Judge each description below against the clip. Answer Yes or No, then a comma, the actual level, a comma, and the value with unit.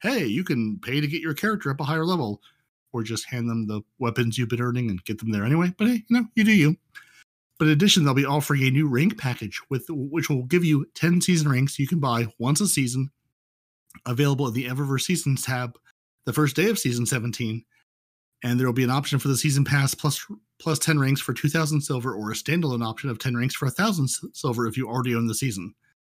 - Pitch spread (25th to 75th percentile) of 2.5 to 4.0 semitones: No, average, 4.4 semitones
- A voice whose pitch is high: No, low, 135 Hz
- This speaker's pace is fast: Yes, fast, 235 wpm